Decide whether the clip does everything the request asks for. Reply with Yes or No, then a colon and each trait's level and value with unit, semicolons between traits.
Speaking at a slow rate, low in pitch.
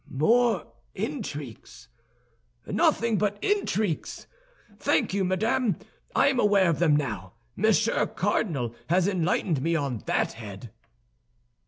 No: slow, 115 wpm; medium, 185 Hz